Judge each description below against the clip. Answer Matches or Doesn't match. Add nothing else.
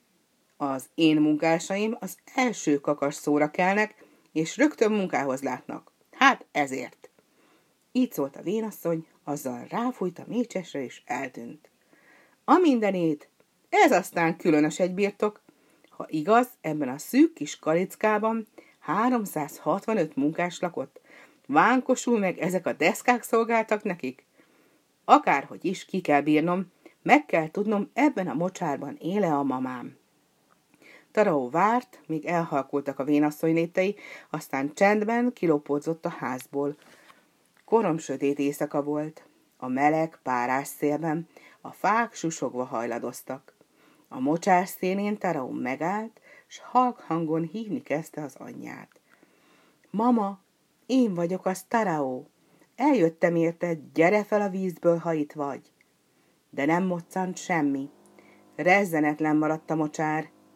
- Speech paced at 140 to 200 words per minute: Doesn't match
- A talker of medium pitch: Matches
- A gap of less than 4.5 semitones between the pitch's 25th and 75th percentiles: Doesn't match